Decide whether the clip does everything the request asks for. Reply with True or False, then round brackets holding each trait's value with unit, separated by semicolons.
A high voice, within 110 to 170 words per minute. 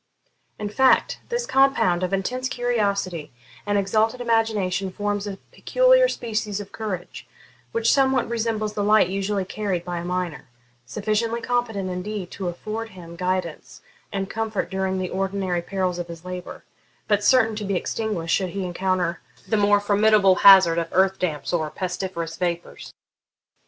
True (195 Hz; 150 wpm)